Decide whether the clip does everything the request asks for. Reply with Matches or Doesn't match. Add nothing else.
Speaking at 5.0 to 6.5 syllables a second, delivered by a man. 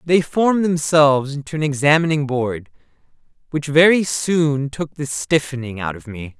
Doesn't match